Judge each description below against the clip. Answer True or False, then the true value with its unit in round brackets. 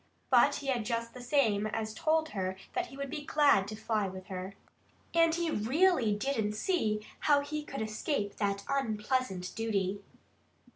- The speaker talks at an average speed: True (165 wpm)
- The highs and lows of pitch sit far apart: True (5.7 semitones)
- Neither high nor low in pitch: False (225 Hz)